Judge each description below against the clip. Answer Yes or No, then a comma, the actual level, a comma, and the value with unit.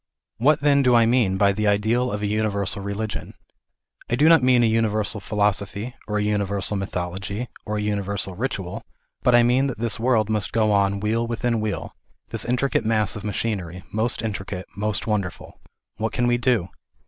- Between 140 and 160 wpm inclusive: No, average, 185 wpm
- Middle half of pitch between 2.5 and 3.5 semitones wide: Yes, average, 2.8 semitones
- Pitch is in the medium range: No, low, 105 Hz